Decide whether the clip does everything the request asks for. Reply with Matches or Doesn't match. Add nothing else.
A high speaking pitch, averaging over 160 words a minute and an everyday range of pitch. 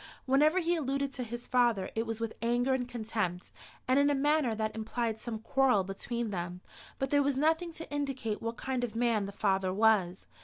Matches